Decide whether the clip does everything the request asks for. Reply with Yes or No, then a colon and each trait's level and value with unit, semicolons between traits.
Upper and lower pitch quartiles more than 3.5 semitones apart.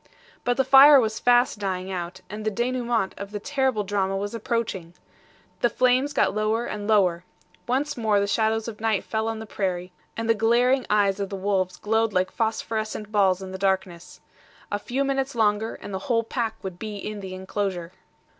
No: average, 3.2 semitones